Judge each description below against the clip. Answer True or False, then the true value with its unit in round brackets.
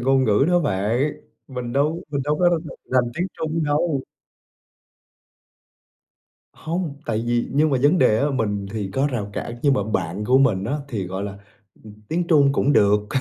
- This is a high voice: False (130 Hz)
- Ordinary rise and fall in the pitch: False (5.9 semitones)